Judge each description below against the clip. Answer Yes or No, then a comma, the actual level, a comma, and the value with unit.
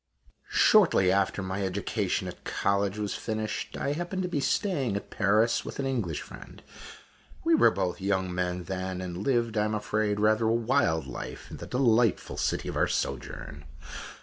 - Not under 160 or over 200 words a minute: Yes, average, 175 wpm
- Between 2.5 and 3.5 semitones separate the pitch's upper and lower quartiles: No, average, 4.1 semitones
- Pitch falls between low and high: No, low, 105 Hz